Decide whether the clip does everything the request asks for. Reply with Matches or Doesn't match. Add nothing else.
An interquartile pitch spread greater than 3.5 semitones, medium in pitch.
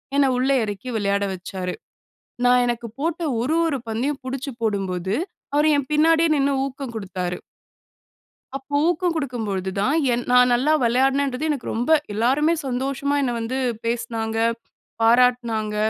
Doesn't match